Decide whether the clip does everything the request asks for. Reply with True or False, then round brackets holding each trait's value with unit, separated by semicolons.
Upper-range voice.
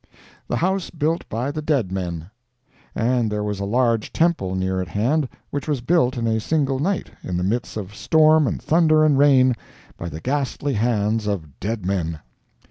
False (120 Hz)